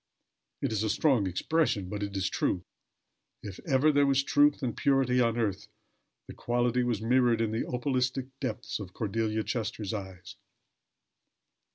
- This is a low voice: Yes, low, 115 Hz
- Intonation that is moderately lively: Yes, average, 3.9 semitones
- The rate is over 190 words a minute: No, average, 155 wpm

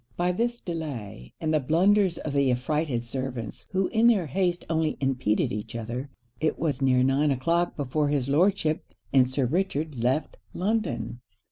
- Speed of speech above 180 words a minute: No, average, 160 wpm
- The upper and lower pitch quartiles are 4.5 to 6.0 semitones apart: Yes, average, 5.2 semitones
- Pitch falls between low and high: Yes, medium, 150 Hz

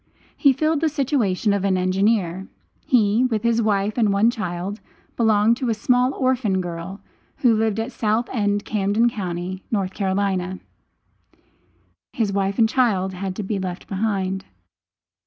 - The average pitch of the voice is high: Yes, high, 205 Hz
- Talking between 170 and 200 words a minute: No, average, 145 wpm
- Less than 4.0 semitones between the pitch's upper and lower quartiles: Yes, average, 3.5 semitones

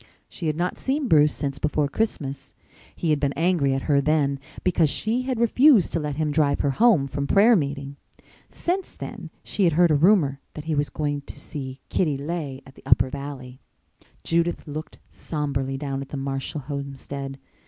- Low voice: No, medium, 145 Hz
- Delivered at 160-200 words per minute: Yes, average, 185 wpm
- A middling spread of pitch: Yes, average, 3.6 semitones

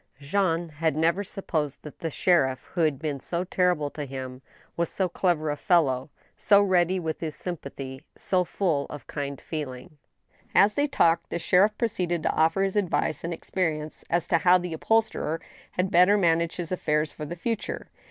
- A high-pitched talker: No, medium, 165 Hz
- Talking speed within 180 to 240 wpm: Yes, average, 190 wpm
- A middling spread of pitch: Yes, average, 3.2 semitones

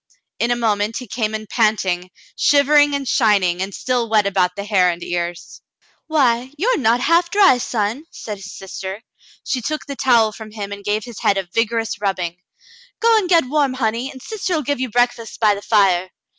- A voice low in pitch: No, high, 225 Hz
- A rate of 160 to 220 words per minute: Yes, average, 200 wpm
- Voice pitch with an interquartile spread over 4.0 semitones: Yes, average, 4.8 semitones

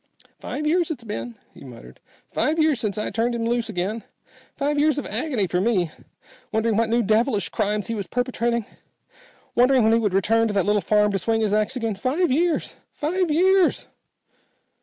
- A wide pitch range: No, average, 5.0 semitones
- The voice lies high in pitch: Yes, high, 230 Hz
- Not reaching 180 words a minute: No, average, 185 wpm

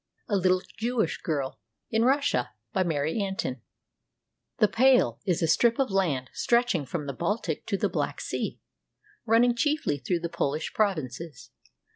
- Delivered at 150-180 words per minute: Yes, average, 155 wpm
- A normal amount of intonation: No, wide, 7.4 semitones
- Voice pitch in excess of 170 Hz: Yes, medium, 185 Hz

